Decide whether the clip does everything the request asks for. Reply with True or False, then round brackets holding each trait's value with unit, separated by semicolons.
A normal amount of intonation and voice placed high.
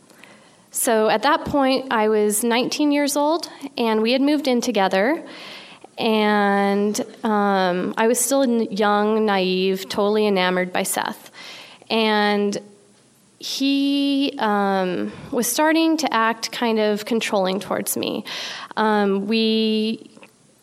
True (4.3 semitones; 220 Hz)